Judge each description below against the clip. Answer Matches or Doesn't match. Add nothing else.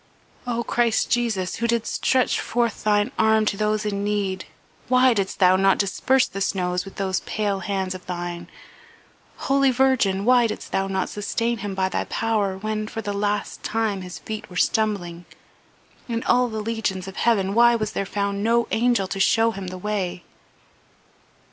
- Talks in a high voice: Matches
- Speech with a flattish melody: Doesn't match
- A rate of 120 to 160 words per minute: Doesn't match